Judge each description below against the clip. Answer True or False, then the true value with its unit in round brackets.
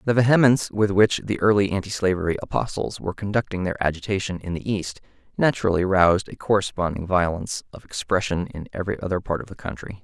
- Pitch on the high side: False (95 Hz)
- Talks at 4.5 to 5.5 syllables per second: False (6.5 syllables/s)